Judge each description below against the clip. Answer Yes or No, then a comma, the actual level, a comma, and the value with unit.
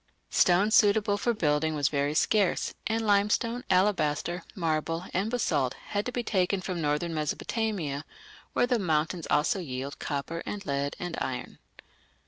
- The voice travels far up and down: Yes, wide, 5.7 semitones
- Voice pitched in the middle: Yes, medium, 175 Hz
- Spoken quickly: No, average, 145 wpm